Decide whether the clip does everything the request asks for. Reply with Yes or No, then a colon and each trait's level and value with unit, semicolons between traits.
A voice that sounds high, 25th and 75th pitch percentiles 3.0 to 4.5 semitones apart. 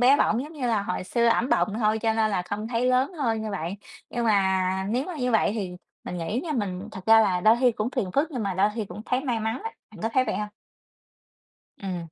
Yes: high, 220 Hz; average, 4.1 semitones